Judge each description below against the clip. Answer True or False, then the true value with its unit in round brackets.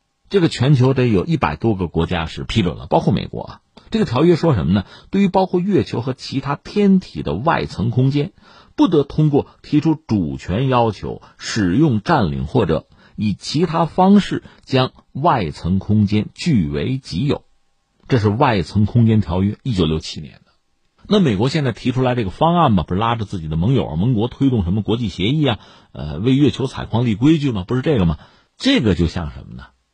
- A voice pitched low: True (120 Hz)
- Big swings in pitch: True (7.5 semitones)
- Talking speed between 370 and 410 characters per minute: False (290 characters per minute)